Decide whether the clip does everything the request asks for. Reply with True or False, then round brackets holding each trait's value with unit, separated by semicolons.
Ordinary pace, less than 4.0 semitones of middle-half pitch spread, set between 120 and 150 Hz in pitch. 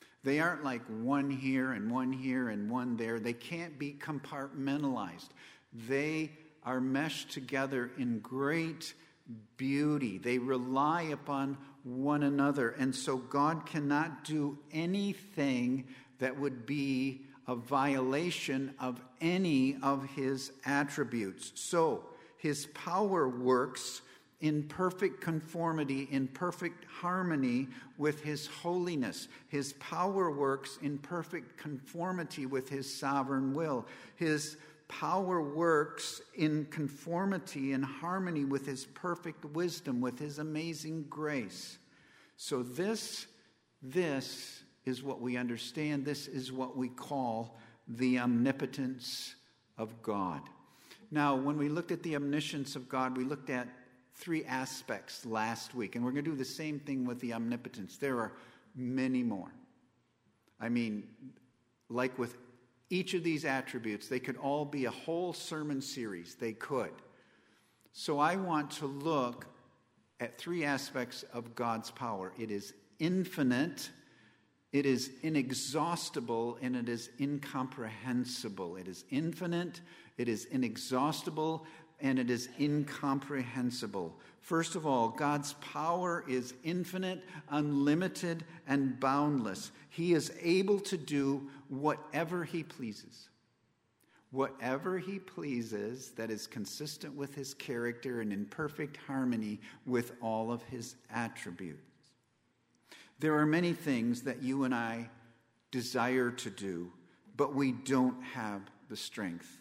False (125 wpm; 3.6 semitones; 135 Hz)